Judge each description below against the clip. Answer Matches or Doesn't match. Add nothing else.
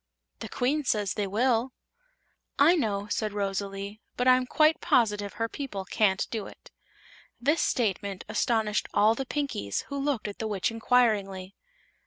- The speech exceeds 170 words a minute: Doesn't match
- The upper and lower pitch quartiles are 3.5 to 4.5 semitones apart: Matches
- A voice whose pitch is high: Matches